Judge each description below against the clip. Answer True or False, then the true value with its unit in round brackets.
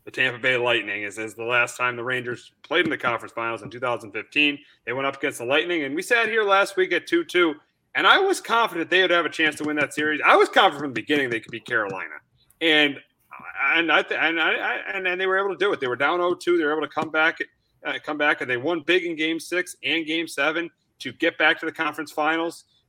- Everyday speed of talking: False (260 wpm)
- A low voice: False (155 Hz)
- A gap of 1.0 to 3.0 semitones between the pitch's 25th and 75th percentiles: False (5.1 semitones)